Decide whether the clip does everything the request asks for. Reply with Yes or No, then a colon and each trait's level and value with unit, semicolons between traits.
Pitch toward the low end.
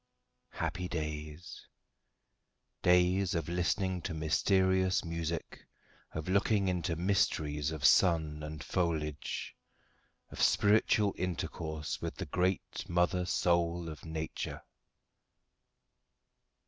Yes: very low, 85 Hz